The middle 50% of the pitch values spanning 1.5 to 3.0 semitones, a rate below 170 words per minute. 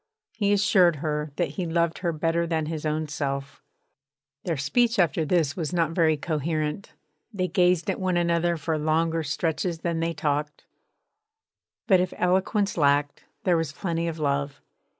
Yes: average, 2.7 semitones; average, 160 wpm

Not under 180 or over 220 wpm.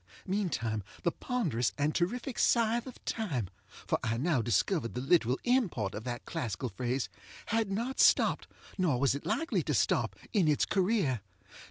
No: average, 160 wpm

